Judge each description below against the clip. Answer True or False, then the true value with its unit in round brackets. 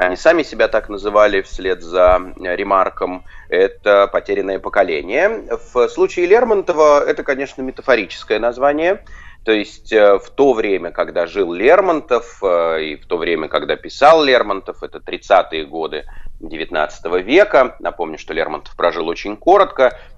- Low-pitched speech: True (110 Hz)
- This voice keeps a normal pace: True (130 wpm)